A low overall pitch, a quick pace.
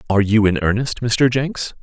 No: low, 115 Hz; average, 195 wpm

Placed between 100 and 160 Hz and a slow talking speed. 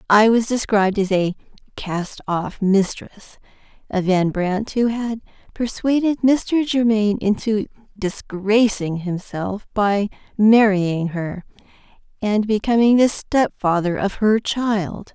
No: high, 210 Hz; slow, 120 wpm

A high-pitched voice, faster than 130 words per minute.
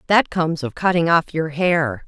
No: medium, 170 Hz; fast, 205 wpm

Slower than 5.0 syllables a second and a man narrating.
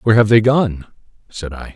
No: 5.4 syllables/s; male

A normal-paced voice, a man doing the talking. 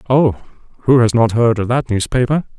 Yes: average, 160 wpm; male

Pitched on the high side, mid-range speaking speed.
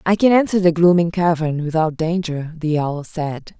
No: medium, 165 Hz; average, 185 wpm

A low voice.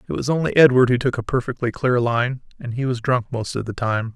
Yes: low, 125 Hz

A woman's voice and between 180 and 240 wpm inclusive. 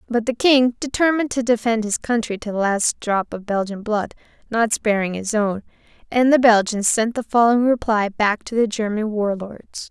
Yes: female; average, 195 wpm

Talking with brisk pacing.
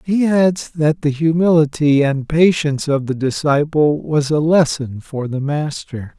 No: average, 155 wpm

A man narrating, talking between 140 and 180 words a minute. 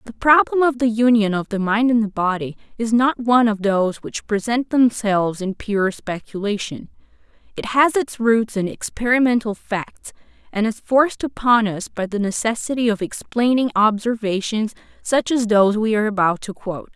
No: female; average, 170 wpm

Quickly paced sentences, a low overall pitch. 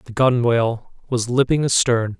No: slow, 135 wpm; low, 120 Hz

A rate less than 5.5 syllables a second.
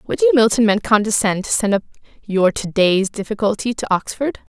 Yes: 5.3 syllables/s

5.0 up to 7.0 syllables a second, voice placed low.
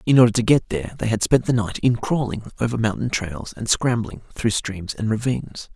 Yes: 5.4 syllables/s; low, 115 Hz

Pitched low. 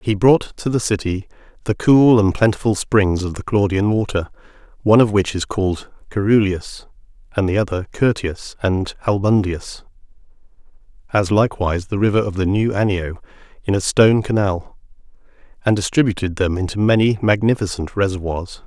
Yes: low, 100 Hz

